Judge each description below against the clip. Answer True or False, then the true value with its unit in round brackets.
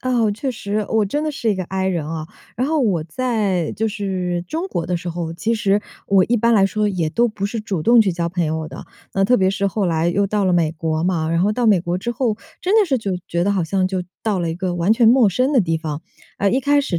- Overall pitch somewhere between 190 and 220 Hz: True (195 Hz)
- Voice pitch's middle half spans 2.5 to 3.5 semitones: False (4.7 semitones)